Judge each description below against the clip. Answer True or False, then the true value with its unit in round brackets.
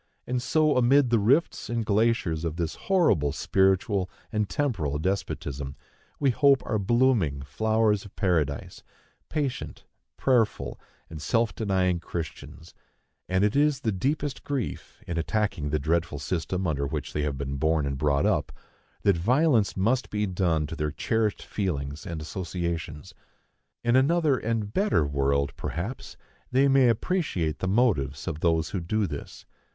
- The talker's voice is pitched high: False (95 Hz)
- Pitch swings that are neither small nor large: False (7.4 semitones)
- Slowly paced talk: False (150 wpm)